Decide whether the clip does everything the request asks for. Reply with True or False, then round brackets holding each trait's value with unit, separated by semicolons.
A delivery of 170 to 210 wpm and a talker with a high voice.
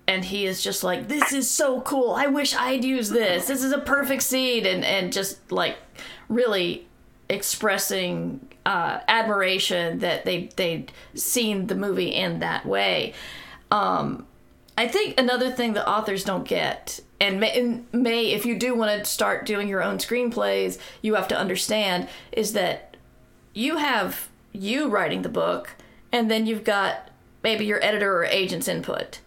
False (160 wpm; 220 Hz)